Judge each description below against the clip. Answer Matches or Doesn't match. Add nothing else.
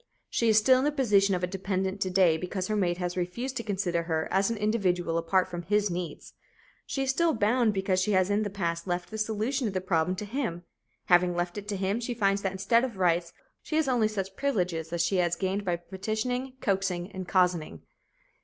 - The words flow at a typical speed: Doesn't match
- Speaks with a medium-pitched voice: Doesn't match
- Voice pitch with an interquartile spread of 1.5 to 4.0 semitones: Matches